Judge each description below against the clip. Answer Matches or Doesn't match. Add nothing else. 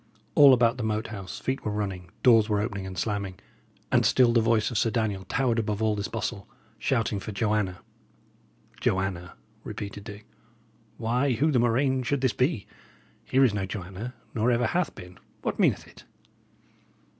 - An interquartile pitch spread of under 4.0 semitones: Matches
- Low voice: Matches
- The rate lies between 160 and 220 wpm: Matches